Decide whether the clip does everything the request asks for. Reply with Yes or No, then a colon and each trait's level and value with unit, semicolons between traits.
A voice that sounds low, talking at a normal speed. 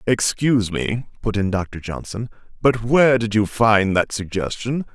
Yes: low, 110 Hz; average, 160 wpm